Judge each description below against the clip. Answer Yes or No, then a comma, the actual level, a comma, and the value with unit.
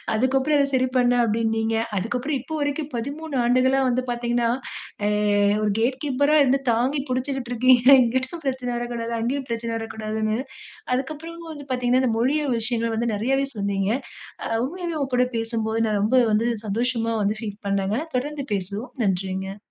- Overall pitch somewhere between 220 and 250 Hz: Yes, high, 245 Hz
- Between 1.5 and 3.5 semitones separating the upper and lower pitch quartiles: Yes, average, 3.2 semitones